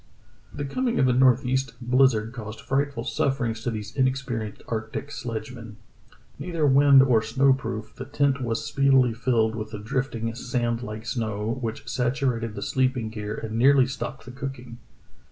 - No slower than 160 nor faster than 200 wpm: Yes, average, 165 wpm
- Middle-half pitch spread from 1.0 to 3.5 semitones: Yes, average, 3.1 semitones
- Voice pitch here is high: No, low, 125 Hz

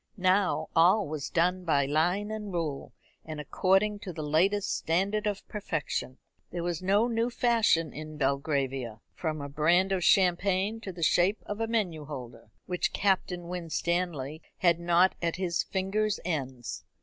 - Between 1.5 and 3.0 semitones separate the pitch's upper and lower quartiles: No, average, 4.1 semitones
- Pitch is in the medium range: Yes, medium, 175 Hz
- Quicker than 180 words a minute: No, average, 155 wpm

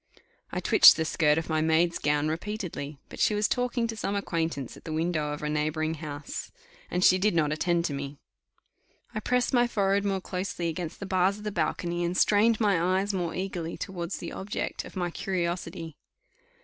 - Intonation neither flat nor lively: Yes, average, 3.9 semitones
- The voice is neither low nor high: Yes, medium, 175 Hz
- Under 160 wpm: No, average, 195 wpm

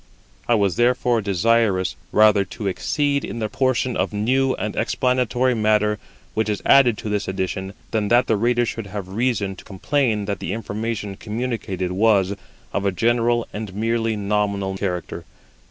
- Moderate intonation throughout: Yes, average, 3.0 semitones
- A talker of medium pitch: No, low, 110 Hz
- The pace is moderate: Yes, average, 160 wpm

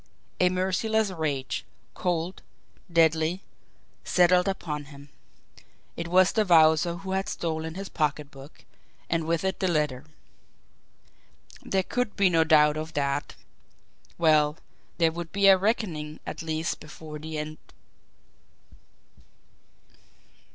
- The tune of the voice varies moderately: Yes, average, 3.2 semitones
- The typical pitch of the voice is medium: Yes, medium, 165 Hz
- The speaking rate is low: Yes, slow, 115 wpm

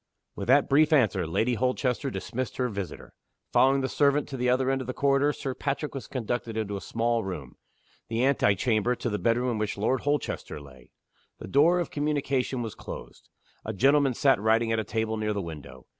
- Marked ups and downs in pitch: No, average, 4.0 semitones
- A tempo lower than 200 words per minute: No, fast, 205 wpm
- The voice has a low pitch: Yes, low, 125 Hz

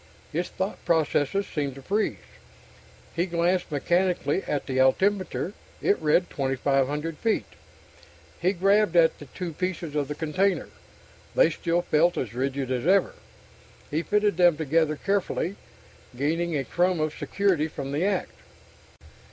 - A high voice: No, medium, 165 Hz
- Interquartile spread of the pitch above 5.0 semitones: No, average, 4.3 semitones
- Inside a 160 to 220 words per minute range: No, average, 140 wpm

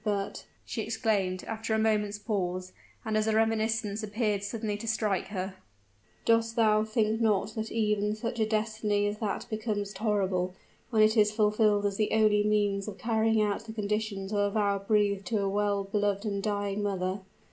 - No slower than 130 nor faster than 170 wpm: No, average, 180 wpm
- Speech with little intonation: Yes, narrow, 1.4 semitones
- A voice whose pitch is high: Yes, high, 210 Hz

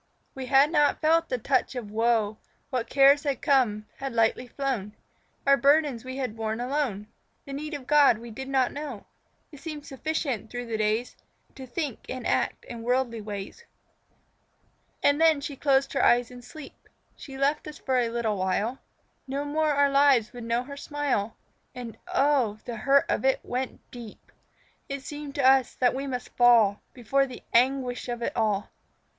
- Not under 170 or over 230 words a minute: Yes, average, 180 wpm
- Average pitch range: Yes, average, 3.3 semitones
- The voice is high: Yes, very high, 260 Hz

